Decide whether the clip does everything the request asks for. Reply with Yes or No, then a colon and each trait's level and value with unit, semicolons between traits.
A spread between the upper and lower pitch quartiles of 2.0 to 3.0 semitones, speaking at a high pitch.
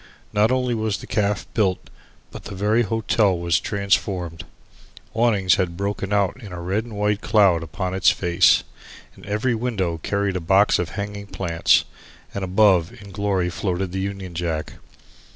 No: narrow, 2.5 semitones; low, 100 Hz